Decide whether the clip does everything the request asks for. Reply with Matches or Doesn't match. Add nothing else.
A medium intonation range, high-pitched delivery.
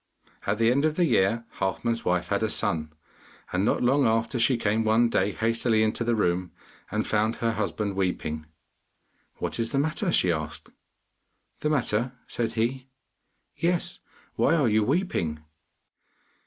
Doesn't match